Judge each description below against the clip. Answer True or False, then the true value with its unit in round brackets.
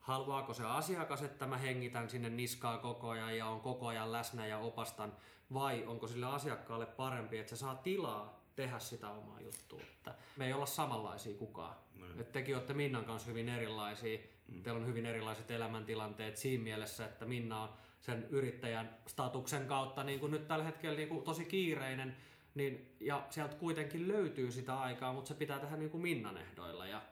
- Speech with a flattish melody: False (3.8 semitones)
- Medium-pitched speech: False (120 Hz)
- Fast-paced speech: True (175 wpm)